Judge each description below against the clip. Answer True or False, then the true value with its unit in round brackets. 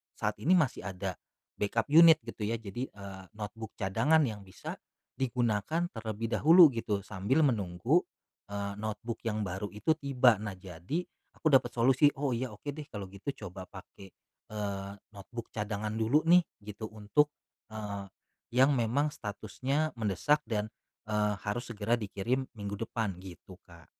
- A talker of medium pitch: False (110 Hz)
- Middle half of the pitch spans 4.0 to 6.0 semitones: True (4.4 semitones)